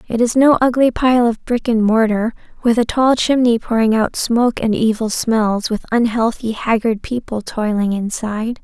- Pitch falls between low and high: No, high, 230 Hz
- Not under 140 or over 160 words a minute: No, average, 175 wpm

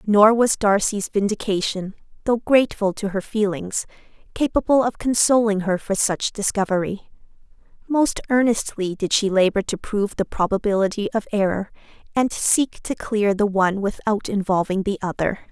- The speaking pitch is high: Yes, high, 205 Hz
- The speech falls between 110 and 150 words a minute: Yes, average, 145 wpm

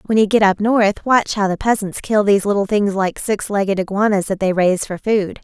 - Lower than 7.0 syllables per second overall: Yes, 5.5 syllables/s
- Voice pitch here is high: Yes, high, 200 Hz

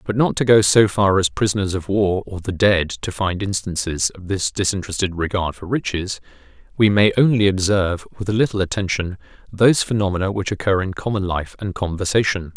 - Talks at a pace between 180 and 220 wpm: Yes, average, 185 wpm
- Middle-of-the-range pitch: No, very low, 95 Hz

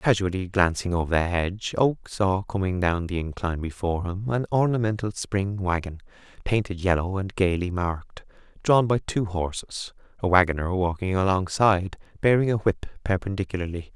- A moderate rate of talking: Yes, average, 145 wpm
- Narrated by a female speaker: No, male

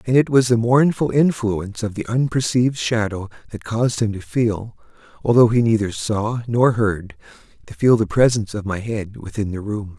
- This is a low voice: Yes, low, 110 Hz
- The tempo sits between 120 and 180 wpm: Yes, average, 175 wpm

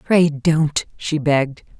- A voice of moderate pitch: Yes, medium, 150 Hz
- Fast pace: No, slow, 135 wpm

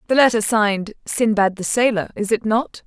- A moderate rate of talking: Yes, average, 190 wpm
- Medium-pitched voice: No, high, 215 Hz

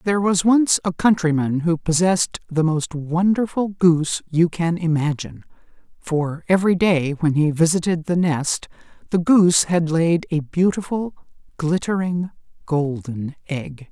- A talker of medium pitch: Yes, medium, 170 Hz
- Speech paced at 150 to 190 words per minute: No, slow, 135 wpm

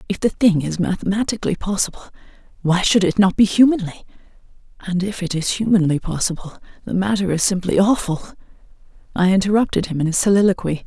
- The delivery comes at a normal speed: Yes, average, 155 wpm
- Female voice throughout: Yes, female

